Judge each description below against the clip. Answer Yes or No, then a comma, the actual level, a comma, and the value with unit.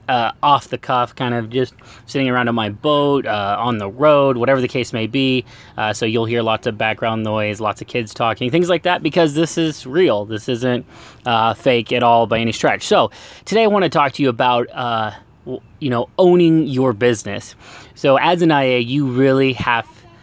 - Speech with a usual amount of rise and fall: Yes, average, 3.3 semitones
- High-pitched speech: No, low, 125 Hz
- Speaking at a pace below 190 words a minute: No, fast, 205 wpm